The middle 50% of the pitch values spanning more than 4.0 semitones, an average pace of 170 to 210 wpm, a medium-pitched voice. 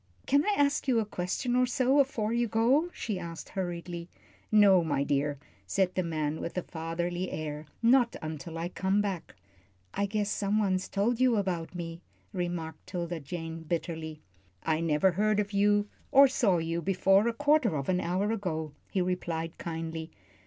Yes: average, 4.5 semitones; average, 175 wpm; medium, 180 Hz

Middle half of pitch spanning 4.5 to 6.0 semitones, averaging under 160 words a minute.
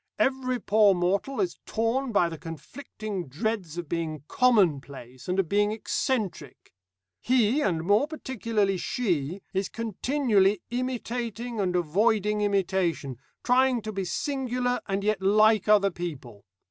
Yes: average, 5.2 semitones; slow, 135 wpm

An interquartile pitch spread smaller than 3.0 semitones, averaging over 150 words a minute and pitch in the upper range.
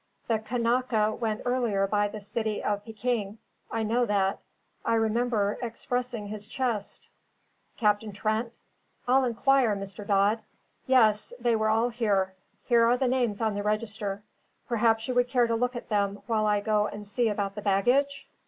Yes: narrow, 2.6 semitones; average, 165 wpm; high, 220 Hz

